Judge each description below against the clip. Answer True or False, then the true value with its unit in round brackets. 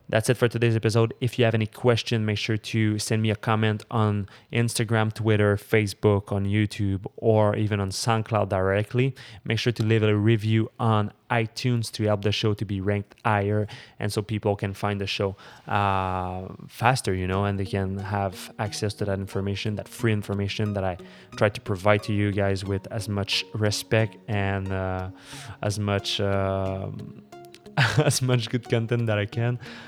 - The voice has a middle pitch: False (105 Hz)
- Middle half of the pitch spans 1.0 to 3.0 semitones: True (2.5 semitones)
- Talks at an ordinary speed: True (180 wpm)